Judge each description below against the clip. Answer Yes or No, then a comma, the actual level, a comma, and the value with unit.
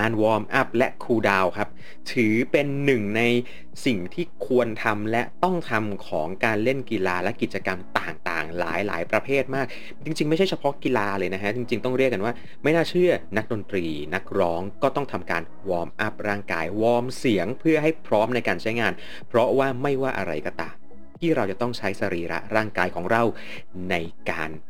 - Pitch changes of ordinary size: No, wide, 6.3 semitones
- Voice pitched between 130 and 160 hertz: No, low, 110 Hz